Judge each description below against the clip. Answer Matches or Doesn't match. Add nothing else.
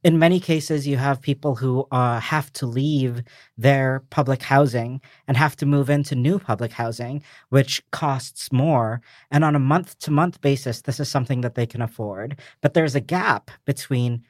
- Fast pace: Doesn't match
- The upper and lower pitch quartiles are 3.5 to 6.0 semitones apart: Doesn't match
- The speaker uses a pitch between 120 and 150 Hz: Matches